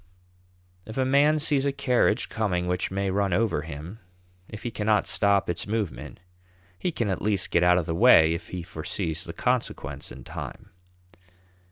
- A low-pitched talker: Yes, low, 100 Hz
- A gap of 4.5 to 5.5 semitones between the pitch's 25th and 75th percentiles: Yes, average, 4.9 semitones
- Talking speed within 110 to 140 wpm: No, average, 175 wpm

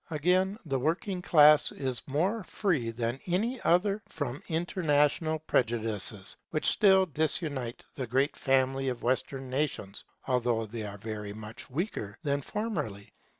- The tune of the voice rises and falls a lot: Yes, wide, 6.3 semitones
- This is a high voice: No, medium, 140 Hz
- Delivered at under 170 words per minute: Yes, slow, 135 wpm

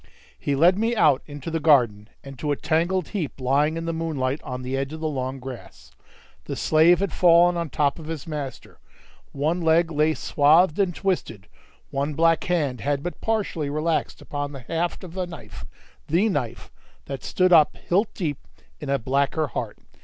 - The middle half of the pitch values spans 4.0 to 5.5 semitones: No, average, 3.6 semitones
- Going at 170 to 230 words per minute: Yes, average, 185 wpm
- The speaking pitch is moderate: Yes, medium, 155 Hz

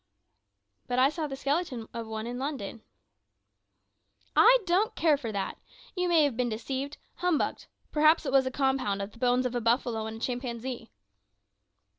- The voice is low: No, very high, 260 Hz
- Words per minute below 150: No, average, 170 wpm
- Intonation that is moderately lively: Yes, average, 4.3 semitones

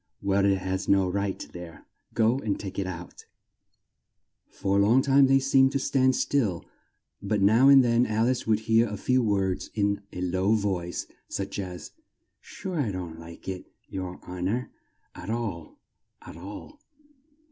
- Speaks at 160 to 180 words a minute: Yes, average, 170 wpm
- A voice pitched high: No, low, 100 Hz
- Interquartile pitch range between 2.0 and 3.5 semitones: No, average, 4.3 semitones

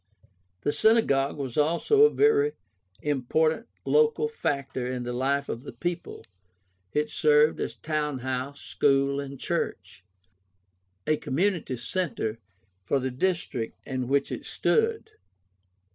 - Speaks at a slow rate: Yes, slow, 130 wpm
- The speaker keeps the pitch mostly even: No, average, 5.2 semitones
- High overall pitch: No, medium, 140 Hz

